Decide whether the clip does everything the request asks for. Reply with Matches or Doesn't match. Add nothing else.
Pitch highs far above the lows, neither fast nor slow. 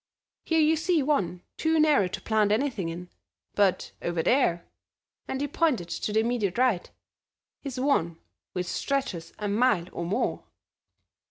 Matches